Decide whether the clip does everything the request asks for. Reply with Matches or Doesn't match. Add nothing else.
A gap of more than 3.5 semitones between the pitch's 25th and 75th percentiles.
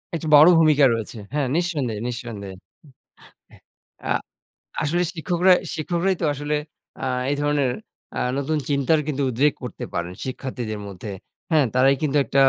Matches